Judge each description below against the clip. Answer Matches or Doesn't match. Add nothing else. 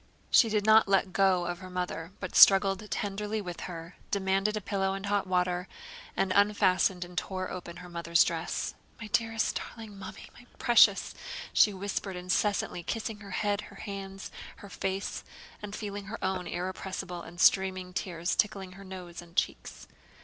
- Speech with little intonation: Matches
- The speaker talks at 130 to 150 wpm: Doesn't match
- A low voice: Doesn't match